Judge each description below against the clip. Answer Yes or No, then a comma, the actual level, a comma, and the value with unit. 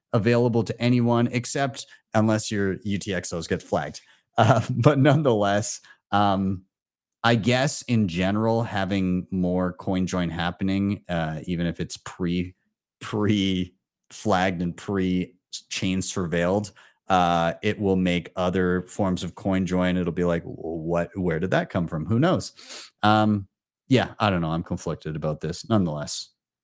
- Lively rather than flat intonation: No, average, 3.5 semitones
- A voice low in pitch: Yes, very low, 95 Hz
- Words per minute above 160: No, average, 140 wpm